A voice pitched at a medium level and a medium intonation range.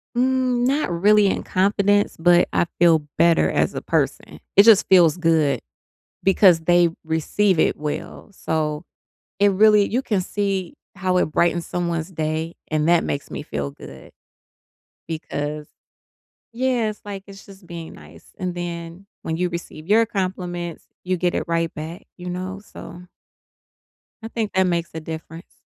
Yes: medium, 175 Hz; average, 3.5 semitones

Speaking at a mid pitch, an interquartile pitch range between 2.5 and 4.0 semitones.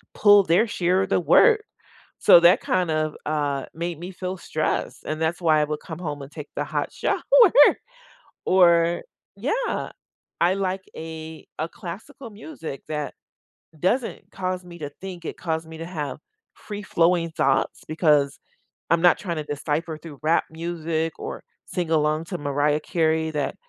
Yes: medium, 165 Hz; average, 2.8 semitones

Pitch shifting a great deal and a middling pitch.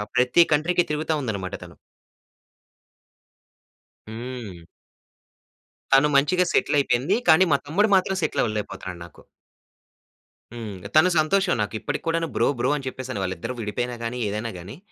No: wide, 6.5 semitones; low, 130 Hz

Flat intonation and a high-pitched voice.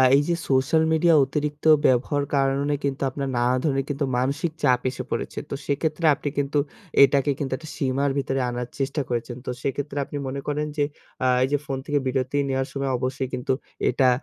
No: narrow, 1.7 semitones; medium, 140 Hz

